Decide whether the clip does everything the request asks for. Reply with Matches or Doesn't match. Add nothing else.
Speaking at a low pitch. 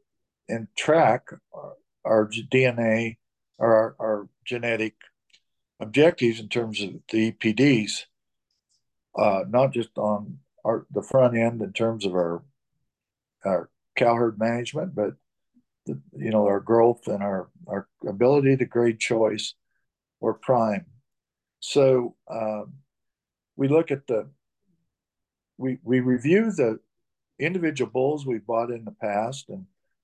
Matches